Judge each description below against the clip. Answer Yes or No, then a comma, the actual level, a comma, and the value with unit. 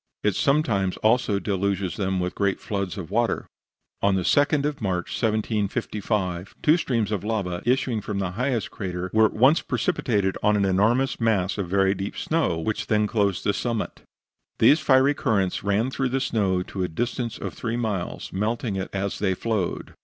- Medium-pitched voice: No, low, 105 Hz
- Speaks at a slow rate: No, average, 180 wpm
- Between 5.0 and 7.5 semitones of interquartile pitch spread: No, average, 3.6 semitones